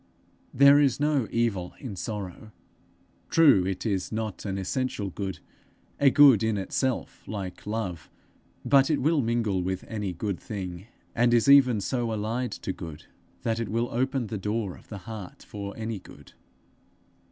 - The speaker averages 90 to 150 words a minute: No, average, 160 wpm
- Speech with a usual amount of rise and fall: Yes, average, 4.2 semitones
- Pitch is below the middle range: Yes, low, 110 Hz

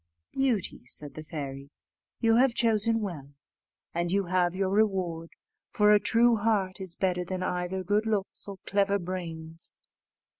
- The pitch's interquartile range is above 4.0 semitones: No, average, 3.5 semitones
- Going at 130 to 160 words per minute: Yes, average, 150 wpm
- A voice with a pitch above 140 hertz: Yes, high, 190 Hz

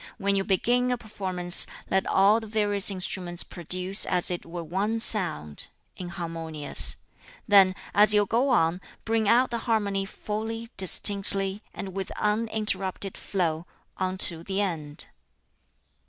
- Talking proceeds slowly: Yes, slow, 130 wpm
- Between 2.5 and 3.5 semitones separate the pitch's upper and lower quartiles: Yes, average, 3.0 semitones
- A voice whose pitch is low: No, high, 195 Hz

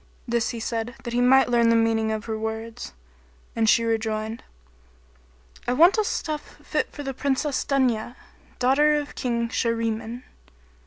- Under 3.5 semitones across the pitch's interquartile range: Yes, average, 2.9 semitones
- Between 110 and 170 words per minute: Yes, average, 155 wpm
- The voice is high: Yes, high, 235 Hz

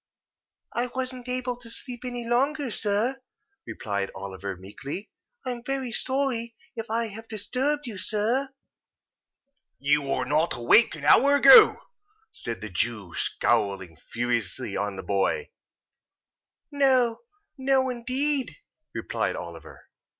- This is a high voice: Yes, high, 230 Hz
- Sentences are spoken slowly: Yes, slow, 120 wpm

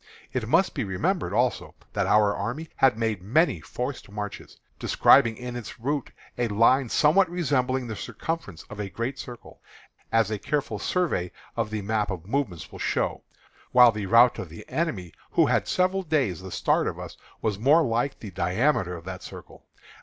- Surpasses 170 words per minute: Yes, average, 180 wpm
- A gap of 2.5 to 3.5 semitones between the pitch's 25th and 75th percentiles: No, wide, 5.5 semitones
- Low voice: Yes, low, 115 Hz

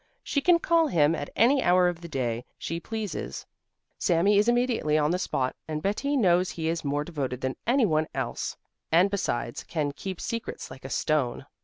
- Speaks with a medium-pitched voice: Yes, medium, 170 Hz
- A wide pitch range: Yes, wide, 6.4 semitones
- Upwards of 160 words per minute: Yes, average, 190 wpm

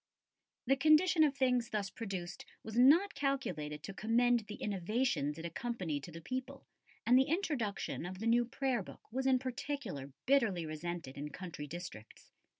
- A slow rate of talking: No, average, 160 wpm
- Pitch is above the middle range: Yes, high, 225 Hz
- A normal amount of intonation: No, wide, 7.3 semitones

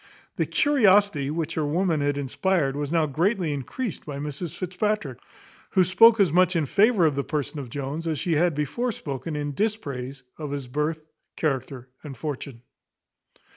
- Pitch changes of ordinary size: Yes, average, 4.6 semitones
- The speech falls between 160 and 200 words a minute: Yes, average, 170 wpm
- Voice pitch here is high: No, medium, 155 Hz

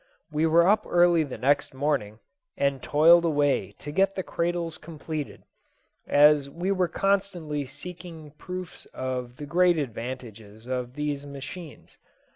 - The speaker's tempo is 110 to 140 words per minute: Yes, slow, 135 wpm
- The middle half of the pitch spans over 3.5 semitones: Yes, average, 4.1 semitones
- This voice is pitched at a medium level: Yes, medium, 150 Hz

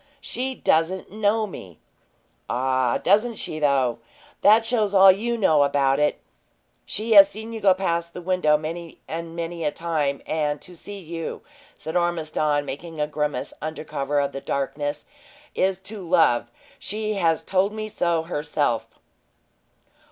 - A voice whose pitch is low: No, medium, 165 Hz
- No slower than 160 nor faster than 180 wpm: No, average, 145 wpm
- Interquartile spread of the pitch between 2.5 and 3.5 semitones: No, average, 5.0 semitones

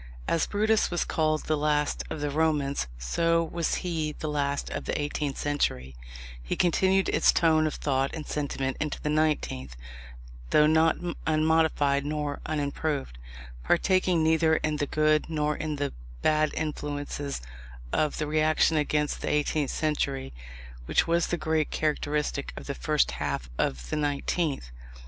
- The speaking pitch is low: No, medium, 150 Hz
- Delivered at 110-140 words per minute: No, average, 150 wpm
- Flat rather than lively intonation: Yes, narrow, 1.7 semitones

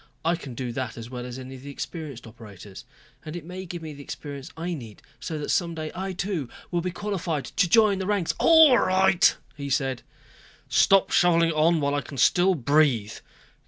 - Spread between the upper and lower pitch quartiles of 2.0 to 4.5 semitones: No, average, 5.3 semitones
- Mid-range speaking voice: Yes, medium, 155 Hz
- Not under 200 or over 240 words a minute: Yes, fast, 205 wpm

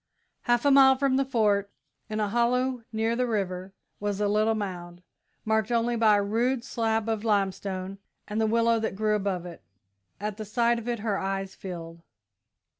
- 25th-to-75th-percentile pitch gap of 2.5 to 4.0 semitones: Yes, average, 3.0 semitones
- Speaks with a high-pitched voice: Yes, high, 215 Hz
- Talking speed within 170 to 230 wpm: Yes, average, 185 wpm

